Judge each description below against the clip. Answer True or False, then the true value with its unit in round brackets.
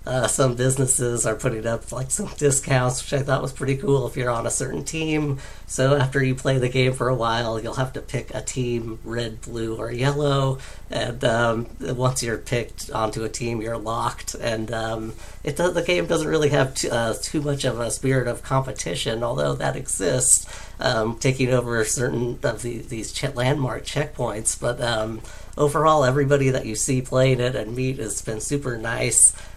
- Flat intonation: False (3.0 semitones)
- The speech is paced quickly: False (195 wpm)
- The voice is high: False (125 Hz)